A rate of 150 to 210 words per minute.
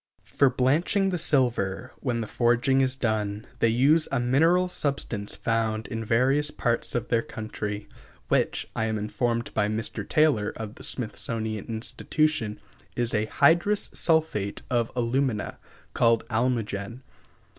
No: slow, 135 wpm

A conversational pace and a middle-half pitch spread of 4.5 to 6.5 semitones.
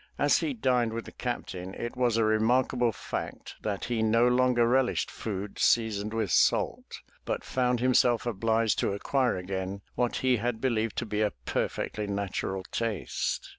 No: average, 165 wpm; average, 2.8 semitones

